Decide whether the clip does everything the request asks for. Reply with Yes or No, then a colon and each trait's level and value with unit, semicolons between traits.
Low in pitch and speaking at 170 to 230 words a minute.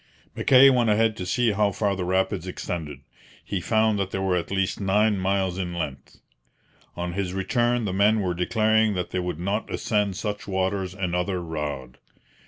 Yes: very low, 95 Hz; average, 180 wpm